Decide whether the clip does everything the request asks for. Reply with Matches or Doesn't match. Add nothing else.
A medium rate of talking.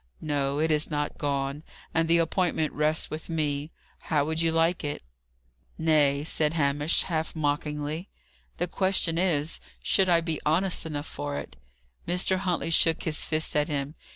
Matches